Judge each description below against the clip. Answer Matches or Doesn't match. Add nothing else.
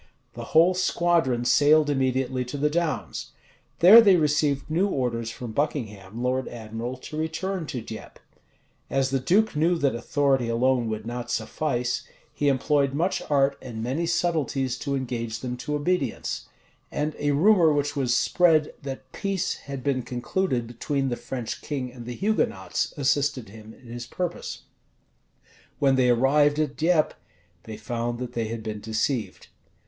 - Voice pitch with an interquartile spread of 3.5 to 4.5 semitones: Matches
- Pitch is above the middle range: Doesn't match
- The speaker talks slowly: Doesn't match